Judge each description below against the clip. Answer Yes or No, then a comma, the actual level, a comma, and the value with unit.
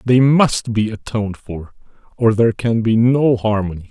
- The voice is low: Yes, low, 110 Hz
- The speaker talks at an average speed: Yes, average, 170 wpm